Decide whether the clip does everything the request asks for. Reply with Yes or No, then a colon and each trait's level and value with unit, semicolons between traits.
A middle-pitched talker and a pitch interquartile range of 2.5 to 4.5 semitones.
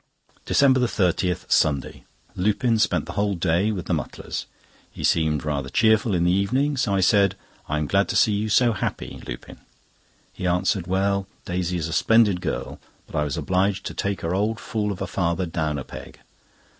No: very low, 95 Hz; average, 3.7 semitones